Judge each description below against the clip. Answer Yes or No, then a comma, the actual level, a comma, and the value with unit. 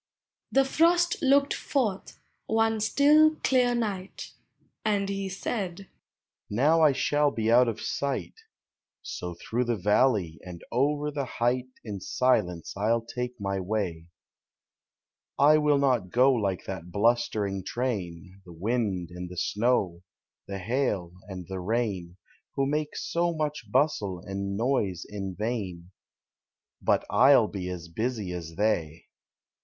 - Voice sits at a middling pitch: No, low, 115 Hz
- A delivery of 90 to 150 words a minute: Yes, average, 140 wpm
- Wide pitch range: Yes, wide, 7.7 semitones